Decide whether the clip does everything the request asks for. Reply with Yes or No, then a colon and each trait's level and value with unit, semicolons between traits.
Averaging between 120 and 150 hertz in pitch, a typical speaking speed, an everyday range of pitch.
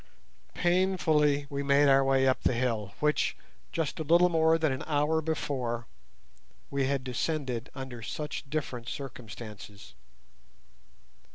No: medium, 140 Hz; slow, 125 wpm; average, 3.8 semitones